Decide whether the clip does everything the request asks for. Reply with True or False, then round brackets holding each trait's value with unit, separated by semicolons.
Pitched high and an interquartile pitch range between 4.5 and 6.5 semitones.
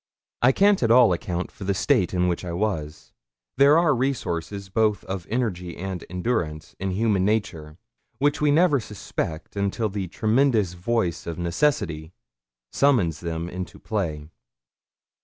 False (95 Hz; 5.5 semitones)